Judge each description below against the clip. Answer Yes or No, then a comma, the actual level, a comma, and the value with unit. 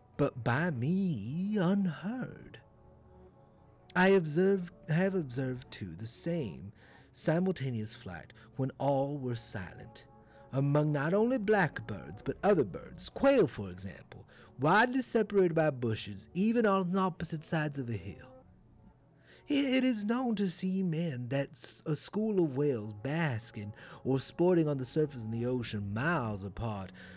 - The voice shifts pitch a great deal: Yes, wide, 7.9 semitones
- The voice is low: No, medium, 145 Hz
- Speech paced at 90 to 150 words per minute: Yes, slow, 135 wpm